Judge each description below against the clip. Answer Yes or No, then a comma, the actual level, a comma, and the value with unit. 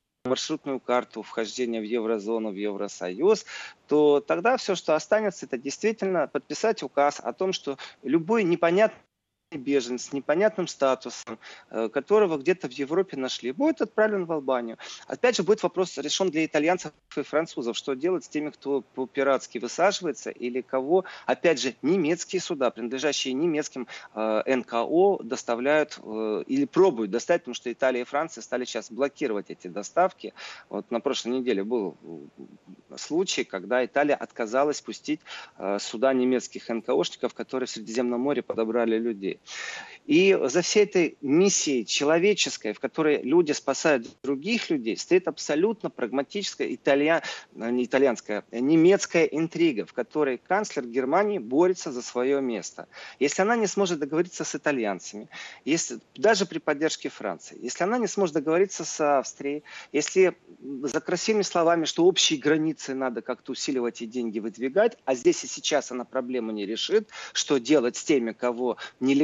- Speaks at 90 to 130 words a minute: No, average, 145 wpm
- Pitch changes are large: Yes, wide, 6.6 semitones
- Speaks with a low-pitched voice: No, medium, 145 Hz